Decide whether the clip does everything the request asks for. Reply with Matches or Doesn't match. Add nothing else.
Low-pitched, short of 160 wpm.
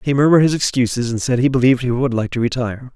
Doesn't match